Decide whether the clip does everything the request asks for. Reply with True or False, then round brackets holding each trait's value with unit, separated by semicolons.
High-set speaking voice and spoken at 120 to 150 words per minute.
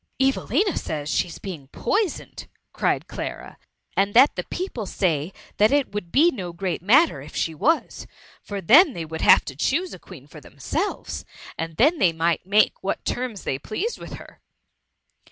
False (200 Hz; 180 wpm)